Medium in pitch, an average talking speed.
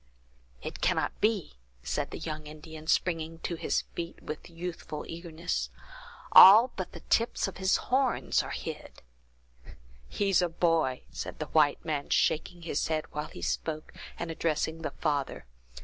Yes: medium, 165 Hz; average, 150 wpm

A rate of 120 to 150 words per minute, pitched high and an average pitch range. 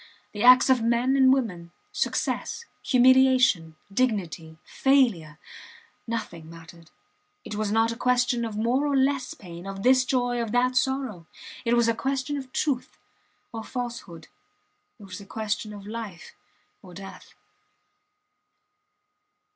Yes: slow, 135 wpm; high, 230 Hz; average, 4.6 semitones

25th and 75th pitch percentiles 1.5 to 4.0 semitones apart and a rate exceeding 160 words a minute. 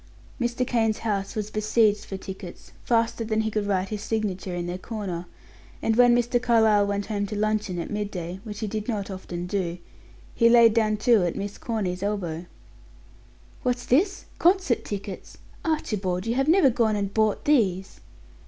Yes: average, 3.1 semitones; average, 170 wpm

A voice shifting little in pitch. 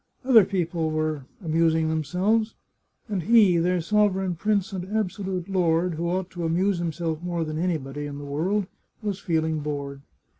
No: average, 3.3 semitones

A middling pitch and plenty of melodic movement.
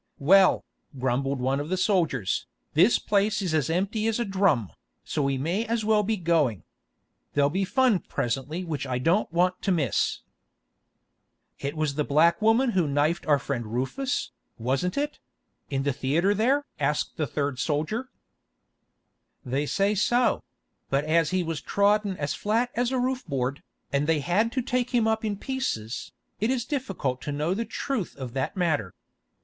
Yes: medium, 170 Hz; wide, 7.4 semitones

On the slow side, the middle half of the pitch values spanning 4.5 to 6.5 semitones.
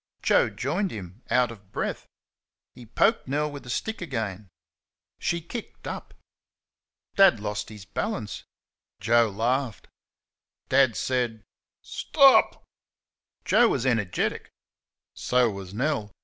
Yes: slow, 120 wpm; wide, 5.6 semitones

